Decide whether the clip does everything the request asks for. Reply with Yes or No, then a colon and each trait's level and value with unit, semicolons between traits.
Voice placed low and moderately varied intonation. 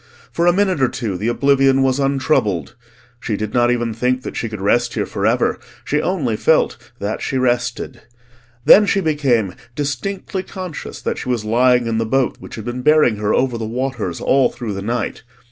Yes: low, 125 Hz; average, 3.5 semitones